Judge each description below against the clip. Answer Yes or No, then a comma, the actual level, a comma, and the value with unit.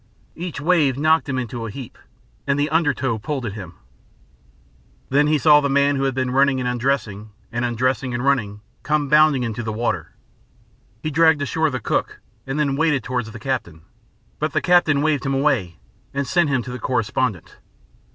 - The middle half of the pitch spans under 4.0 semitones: Yes, average, 3.6 semitones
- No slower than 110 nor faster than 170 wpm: No, average, 190 wpm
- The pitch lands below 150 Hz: Yes, low, 135 Hz